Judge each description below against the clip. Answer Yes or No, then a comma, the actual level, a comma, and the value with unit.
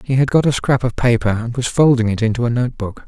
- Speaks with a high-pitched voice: No, low, 120 Hz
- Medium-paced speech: No, fast, 290 wpm